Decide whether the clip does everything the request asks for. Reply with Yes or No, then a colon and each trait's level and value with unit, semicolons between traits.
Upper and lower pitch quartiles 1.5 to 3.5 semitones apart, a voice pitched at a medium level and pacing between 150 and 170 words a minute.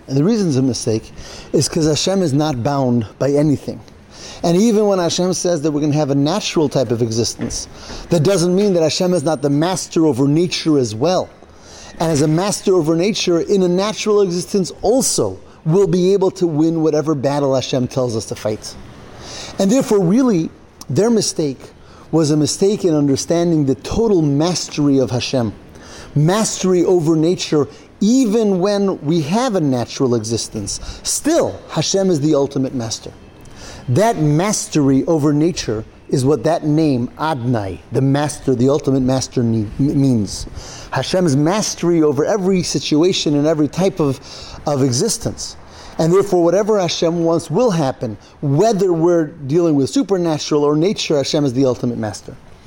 No: average, 5.1 semitones; medium, 155 Hz; average, 160 wpm